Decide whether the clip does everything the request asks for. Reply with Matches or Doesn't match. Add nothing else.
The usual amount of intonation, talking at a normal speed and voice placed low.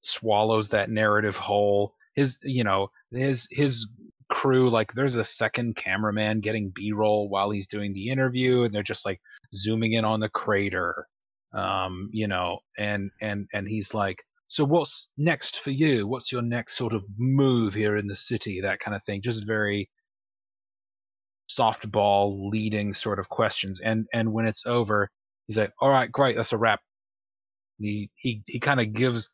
Matches